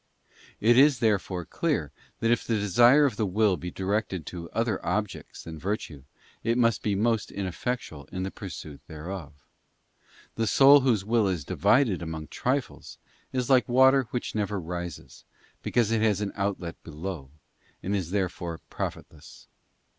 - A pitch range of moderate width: Yes, average, 4.9 semitones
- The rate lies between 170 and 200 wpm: No, average, 155 wpm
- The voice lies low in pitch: Yes, low, 100 Hz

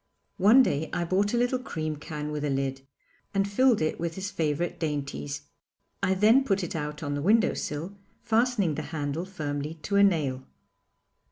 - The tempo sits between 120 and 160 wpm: No, average, 180 wpm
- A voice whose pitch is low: No, medium, 165 Hz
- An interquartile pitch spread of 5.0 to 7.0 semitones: Yes, average, 5.3 semitones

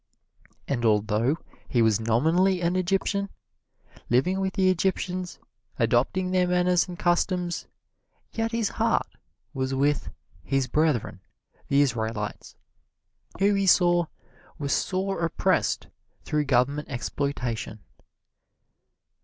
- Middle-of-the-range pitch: Yes, medium, 160 Hz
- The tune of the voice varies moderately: No, wide, 6.8 semitones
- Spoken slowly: Yes, slow, 105 wpm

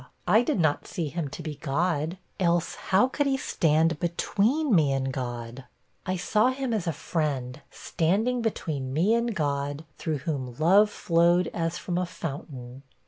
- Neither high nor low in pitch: Yes, medium, 165 Hz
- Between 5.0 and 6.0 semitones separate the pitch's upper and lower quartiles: Yes, wide, 5.4 semitones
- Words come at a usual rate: Yes, average, 165 wpm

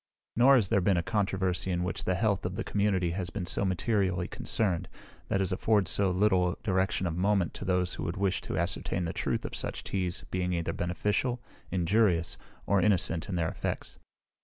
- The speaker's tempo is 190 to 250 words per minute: Yes, average, 195 wpm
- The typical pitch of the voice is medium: No, very low, 95 Hz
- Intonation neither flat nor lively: No, narrow, 2.3 semitones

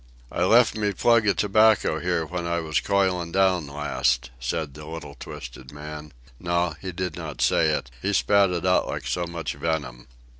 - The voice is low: Yes, very low, 85 Hz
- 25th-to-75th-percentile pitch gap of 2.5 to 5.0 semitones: Yes, average, 4.2 semitones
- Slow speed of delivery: No, average, 180 wpm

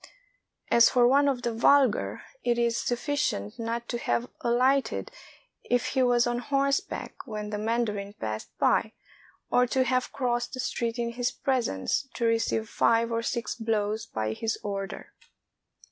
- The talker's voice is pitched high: Yes, high, 235 Hz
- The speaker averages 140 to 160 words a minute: Yes, average, 155 wpm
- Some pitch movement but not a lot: No, narrow, 2.0 semitones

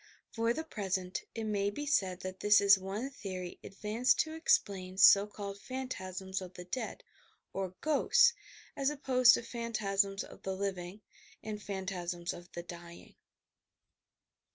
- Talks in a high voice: Yes, high, 200 Hz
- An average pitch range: Yes, average, 3.8 semitones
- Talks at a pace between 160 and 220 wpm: No, average, 150 wpm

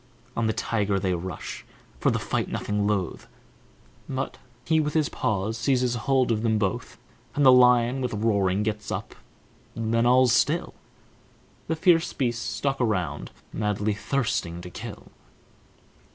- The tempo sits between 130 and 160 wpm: Yes, average, 145 wpm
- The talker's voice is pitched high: No, low, 115 Hz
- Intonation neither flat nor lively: Yes, average, 3.8 semitones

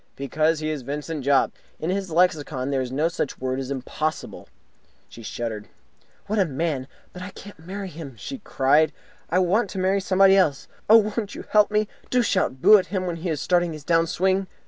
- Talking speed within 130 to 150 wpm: No, fast, 205 wpm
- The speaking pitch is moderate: Yes, medium, 165 Hz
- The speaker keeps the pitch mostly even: No, average, 5.2 semitones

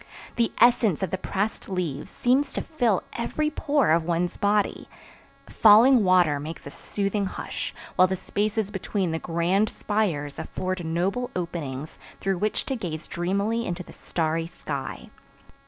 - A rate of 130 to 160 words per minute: Yes, average, 150 wpm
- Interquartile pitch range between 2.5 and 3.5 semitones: No, average, 4.4 semitones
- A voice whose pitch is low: No, high, 190 Hz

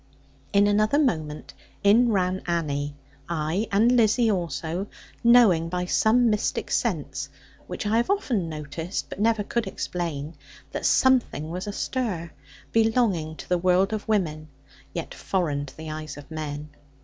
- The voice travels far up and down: Yes, wide, 5.7 semitones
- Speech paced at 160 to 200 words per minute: No, average, 145 wpm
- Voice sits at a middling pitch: Yes, medium, 180 Hz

